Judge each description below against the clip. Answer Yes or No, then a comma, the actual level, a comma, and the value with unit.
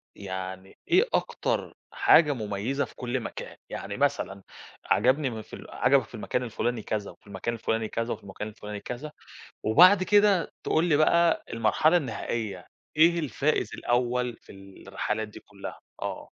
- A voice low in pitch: Yes, low, 120 Hz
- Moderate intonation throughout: No, wide, 6.3 semitones